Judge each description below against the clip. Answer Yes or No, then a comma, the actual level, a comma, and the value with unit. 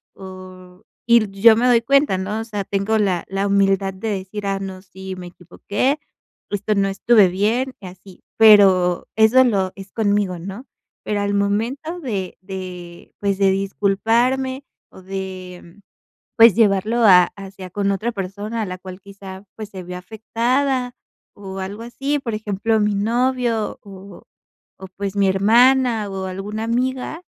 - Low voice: No, high, 200 Hz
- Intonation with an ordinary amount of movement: Yes, average, 3.1 semitones